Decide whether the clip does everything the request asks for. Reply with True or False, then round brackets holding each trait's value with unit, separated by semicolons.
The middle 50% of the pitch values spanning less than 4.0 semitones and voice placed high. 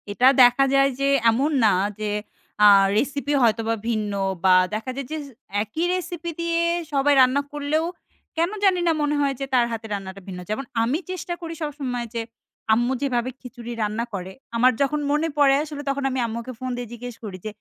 False (4.3 semitones; 255 Hz)